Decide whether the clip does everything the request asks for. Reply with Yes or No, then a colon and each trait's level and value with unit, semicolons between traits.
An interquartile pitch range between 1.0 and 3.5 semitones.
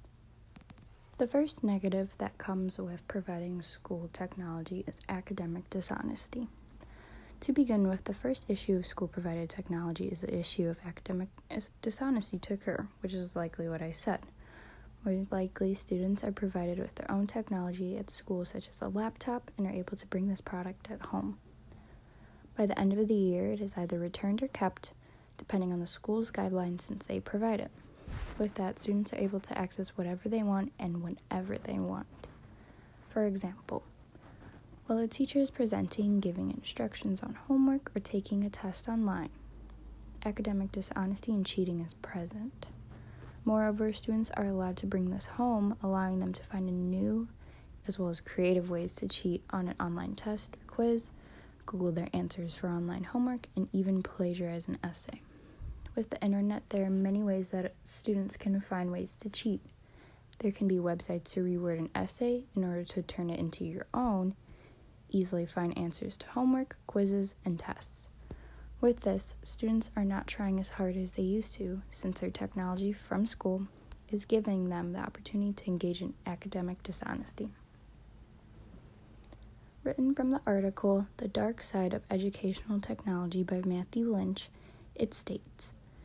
Yes: average, 2.8 semitones